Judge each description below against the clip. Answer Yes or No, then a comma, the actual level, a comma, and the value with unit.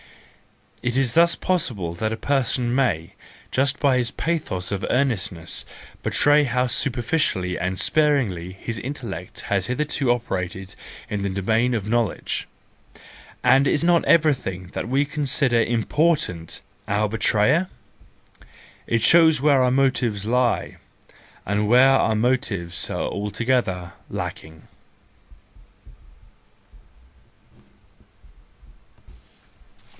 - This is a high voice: No, low, 120 Hz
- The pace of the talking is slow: Yes, slow, 105 wpm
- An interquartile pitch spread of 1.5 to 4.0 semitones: No, wide, 5.6 semitones